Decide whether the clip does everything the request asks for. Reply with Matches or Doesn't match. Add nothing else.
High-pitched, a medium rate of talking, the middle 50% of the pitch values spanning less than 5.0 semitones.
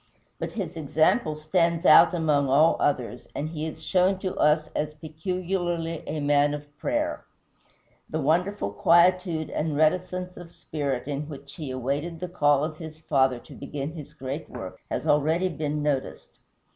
Doesn't match